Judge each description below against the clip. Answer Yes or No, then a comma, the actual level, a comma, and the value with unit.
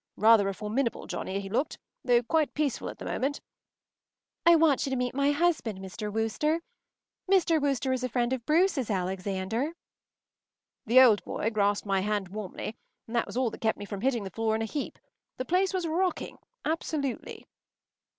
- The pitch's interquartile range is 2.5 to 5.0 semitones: No, wide, 5.6 semitones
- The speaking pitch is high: Yes, high, 240 Hz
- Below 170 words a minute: No, average, 180 wpm